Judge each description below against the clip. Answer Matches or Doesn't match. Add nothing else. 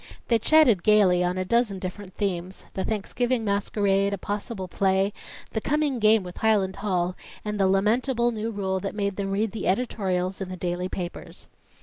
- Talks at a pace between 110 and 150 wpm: Doesn't match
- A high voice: Matches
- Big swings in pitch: Doesn't match